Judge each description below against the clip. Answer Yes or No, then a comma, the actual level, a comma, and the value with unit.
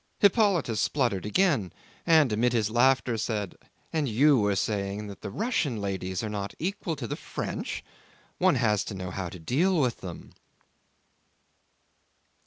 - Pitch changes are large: Yes, wide, 6.8 semitones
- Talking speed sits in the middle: Yes, average, 150 wpm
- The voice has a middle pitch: No, low, 110 Hz